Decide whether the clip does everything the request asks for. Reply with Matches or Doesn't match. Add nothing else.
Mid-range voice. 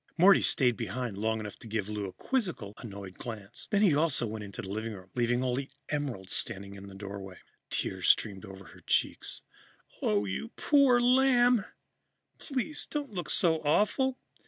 Doesn't match